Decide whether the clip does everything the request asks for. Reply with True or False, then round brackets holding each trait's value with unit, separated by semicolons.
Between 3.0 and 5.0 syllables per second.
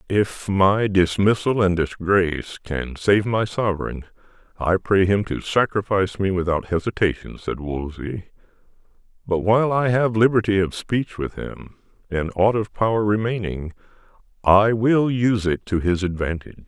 True (4.8 syllables/s)